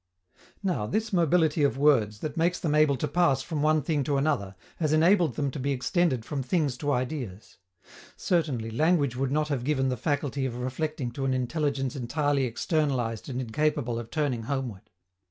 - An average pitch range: Yes, average, 3.6 semitones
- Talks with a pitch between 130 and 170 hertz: Yes, medium, 140 Hz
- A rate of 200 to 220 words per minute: No, average, 180 wpm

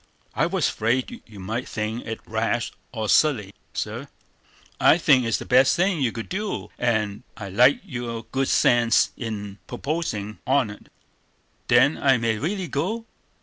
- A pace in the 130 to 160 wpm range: Yes, average, 150 wpm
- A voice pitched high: No, low, 120 Hz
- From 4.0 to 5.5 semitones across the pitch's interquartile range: Yes, average, 4.3 semitones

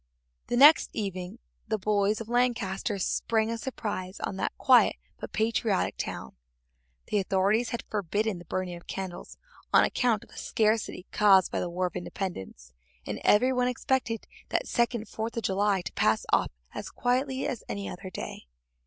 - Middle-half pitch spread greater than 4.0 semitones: No, average, 3.7 semitones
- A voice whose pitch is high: Yes, high, 210 Hz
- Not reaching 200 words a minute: Yes, average, 170 wpm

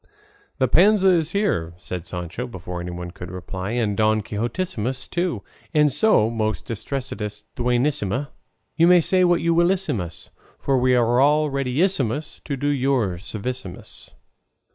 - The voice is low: Yes, low, 125 Hz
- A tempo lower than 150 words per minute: Yes, average, 140 wpm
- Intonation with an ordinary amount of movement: No, wide, 6.7 semitones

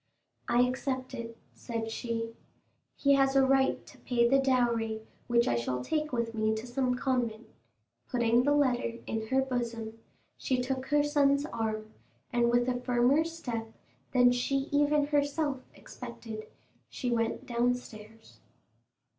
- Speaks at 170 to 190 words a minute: No, average, 145 wpm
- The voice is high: Yes, high, 245 Hz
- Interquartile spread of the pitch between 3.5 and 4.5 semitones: No, average, 2.9 semitones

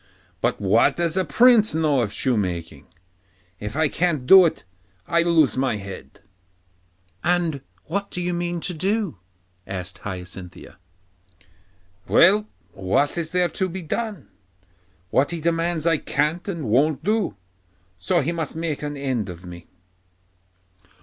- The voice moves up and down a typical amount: No, wide, 7.6 semitones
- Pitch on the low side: No, medium, 155 Hz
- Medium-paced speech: Yes, average, 145 wpm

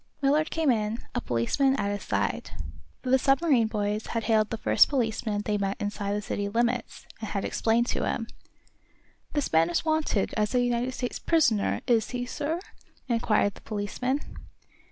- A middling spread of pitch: Yes, average, 3.8 semitones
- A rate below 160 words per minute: No, average, 175 wpm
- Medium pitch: No, high, 230 Hz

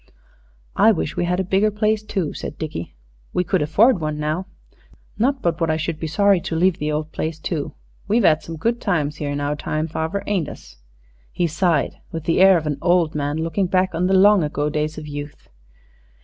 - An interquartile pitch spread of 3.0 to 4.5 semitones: Yes, average, 3.8 semitones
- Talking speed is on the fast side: Yes, fast, 215 wpm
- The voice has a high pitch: No, medium, 165 Hz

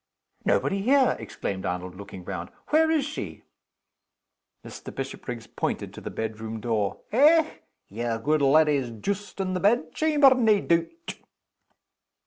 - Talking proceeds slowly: Yes, slow, 125 wpm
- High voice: No, medium, 155 Hz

